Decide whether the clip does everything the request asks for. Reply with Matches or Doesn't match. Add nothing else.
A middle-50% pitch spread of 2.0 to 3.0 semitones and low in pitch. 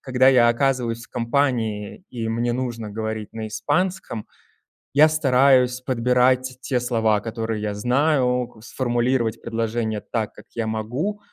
Matches